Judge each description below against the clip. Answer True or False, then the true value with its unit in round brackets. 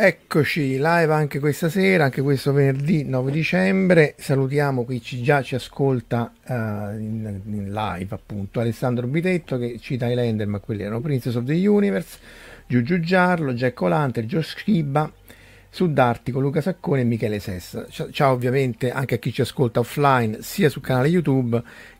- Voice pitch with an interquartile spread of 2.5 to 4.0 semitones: False (4.6 semitones)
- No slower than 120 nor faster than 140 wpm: False (160 wpm)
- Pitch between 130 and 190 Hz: True (135 Hz)